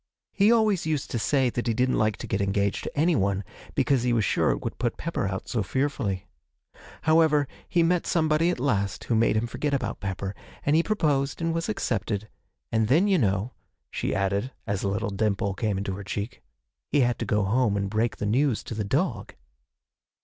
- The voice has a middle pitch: No, low, 120 Hz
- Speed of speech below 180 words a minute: No, fast, 205 wpm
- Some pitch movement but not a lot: No, wide, 6.7 semitones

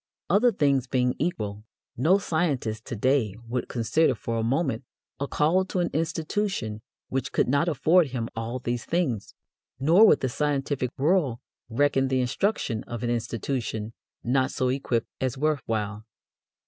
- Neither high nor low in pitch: No, low, 130 Hz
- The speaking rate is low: No, average, 160 wpm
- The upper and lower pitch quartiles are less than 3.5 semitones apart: No, average, 5.0 semitones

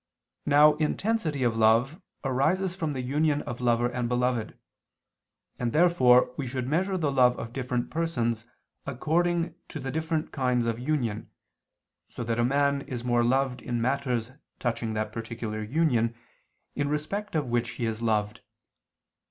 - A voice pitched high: No, low, 125 Hz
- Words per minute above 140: Yes, average, 150 wpm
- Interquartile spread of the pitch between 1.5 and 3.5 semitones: No, average, 4.3 semitones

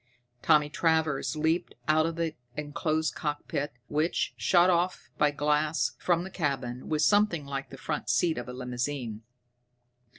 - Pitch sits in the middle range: Yes, medium, 150 Hz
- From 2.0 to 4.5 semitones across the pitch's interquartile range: Yes, average, 2.9 semitones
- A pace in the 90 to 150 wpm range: Yes, average, 145 wpm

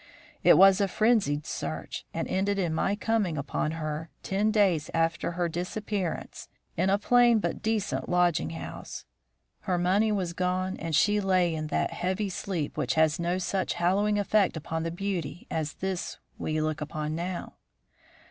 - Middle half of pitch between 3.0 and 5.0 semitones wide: Yes, average, 3.8 semitones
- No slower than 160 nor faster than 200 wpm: Yes, average, 165 wpm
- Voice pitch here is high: No, medium, 180 Hz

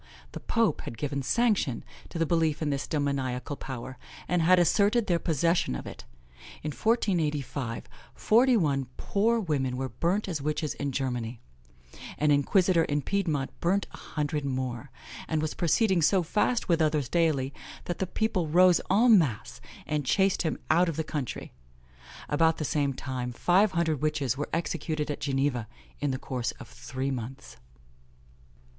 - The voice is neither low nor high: Yes, medium, 150 Hz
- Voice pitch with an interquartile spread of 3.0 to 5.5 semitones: Yes, average, 4.8 semitones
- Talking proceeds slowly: No, average, 160 wpm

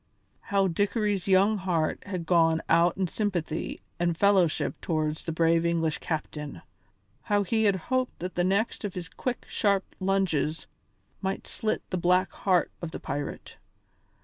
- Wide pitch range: No, average, 3.4 semitones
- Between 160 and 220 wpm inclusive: No, average, 150 wpm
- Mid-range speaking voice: Yes, medium, 180 Hz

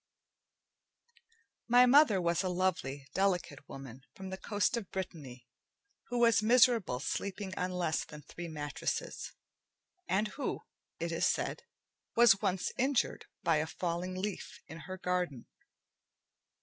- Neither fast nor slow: No, slow, 130 wpm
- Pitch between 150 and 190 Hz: Yes, medium, 185 Hz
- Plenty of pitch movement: No, average, 4.6 semitones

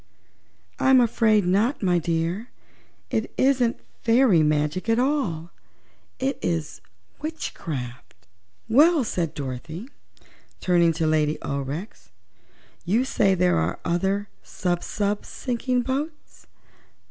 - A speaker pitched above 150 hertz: Yes, high, 190 Hz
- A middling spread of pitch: No, wide, 7.0 semitones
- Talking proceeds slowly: Yes, slow, 105 wpm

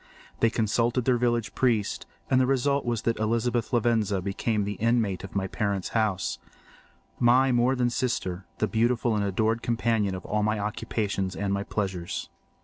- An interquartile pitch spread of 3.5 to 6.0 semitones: No, average, 3.0 semitones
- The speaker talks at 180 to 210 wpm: No, average, 155 wpm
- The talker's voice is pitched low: Yes, low, 110 Hz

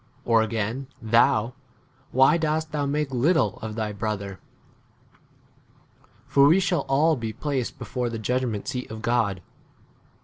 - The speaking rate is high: No, average, 140 wpm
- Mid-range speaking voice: No, low, 120 Hz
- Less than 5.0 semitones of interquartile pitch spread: Yes, average, 4.6 semitones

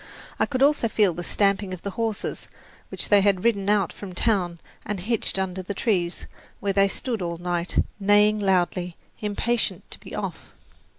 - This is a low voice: No, high, 200 Hz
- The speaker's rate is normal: Yes, average, 175 wpm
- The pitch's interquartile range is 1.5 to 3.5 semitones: Yes, narrow, 2.6 semitones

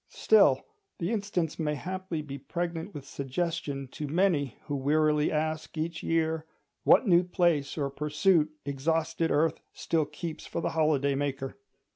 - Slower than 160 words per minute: Yes, average, 145 wpm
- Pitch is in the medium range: Yes, medium, 155 Hz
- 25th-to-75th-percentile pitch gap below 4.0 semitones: Yes, average, 2.8 semitones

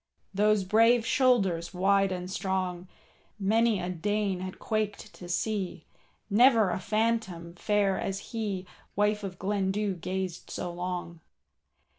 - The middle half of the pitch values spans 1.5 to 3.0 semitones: Yes, average, 2.7 semitones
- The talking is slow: Yes, slow, 125 wpm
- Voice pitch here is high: Yes, high, 195 Hz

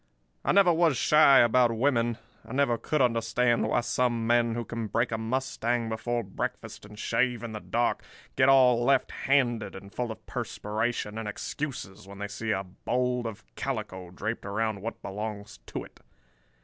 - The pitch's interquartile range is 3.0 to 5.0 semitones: No, narrow, 2.6 semitones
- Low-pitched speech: Yes, low, 115 Hz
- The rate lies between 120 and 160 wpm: No, average, 175 wpm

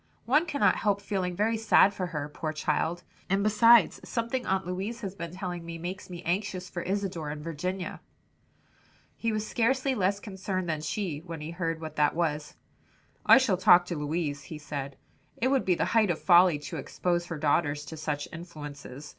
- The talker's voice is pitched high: No, medium, 180 Hz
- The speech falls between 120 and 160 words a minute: No, average, 190 wpm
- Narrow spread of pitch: No, average, 4.3 semitones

